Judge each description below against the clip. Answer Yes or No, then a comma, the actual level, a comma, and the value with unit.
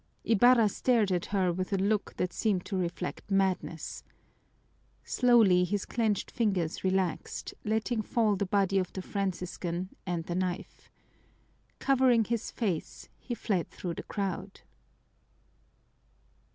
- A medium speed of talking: No, slow, 125 wpm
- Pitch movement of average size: Yes, average, 3.3 semitones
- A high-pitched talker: Yes, high, 195 Hz